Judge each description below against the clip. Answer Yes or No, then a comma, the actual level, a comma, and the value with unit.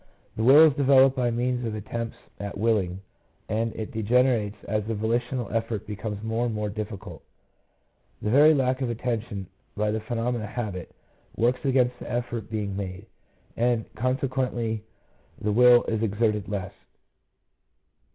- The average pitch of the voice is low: Yes, low, 115 Hz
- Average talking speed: Yes, average, 150 wpm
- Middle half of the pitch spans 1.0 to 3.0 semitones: Yes, average, 2.7 semitones